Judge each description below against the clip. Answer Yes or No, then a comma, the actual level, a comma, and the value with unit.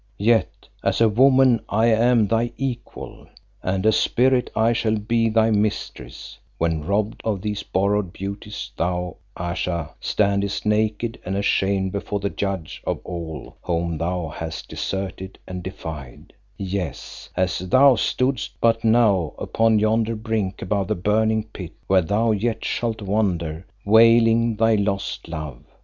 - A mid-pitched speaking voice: No, low, 105 Hz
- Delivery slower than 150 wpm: Yes, average, 140 wpm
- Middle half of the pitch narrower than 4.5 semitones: Yes, average, 3.5 semitones